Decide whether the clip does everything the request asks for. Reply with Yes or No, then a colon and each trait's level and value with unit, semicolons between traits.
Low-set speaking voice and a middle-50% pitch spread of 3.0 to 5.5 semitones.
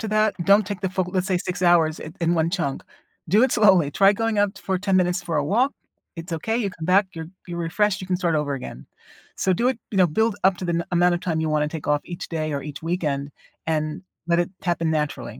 No: medium, 175 Hz; average, 3.6 semitones